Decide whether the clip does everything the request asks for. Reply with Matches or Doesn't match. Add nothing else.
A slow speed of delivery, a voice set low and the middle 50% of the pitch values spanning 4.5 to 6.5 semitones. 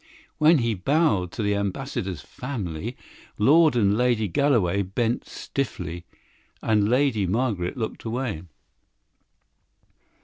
Matches